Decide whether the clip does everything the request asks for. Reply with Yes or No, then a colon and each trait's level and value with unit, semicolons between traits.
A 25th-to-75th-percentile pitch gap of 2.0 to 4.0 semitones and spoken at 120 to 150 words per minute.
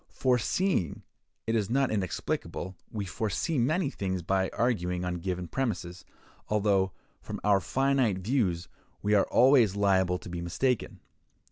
No: wide, 5.4 semitones; average, 140 wpm